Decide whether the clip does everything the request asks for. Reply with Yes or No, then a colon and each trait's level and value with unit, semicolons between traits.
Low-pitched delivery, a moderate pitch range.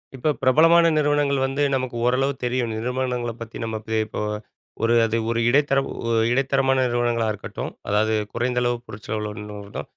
Yes: low, 120 Hz; average, 3.1 semitones